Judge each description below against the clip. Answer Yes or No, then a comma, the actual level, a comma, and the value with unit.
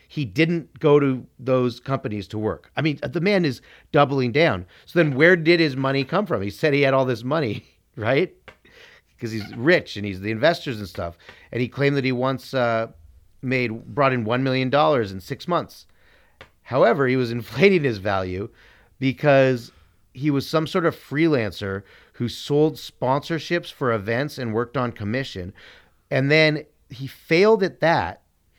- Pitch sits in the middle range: No, low, 130 Hz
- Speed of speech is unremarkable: Yes, average, 175 wpm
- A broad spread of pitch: No, average, 4.8 semitones